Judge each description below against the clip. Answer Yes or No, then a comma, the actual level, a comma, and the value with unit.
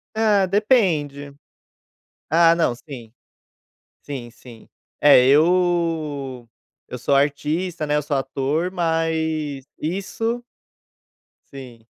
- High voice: No, medium, 150 Hz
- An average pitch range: Yes, average, 4.0 semitones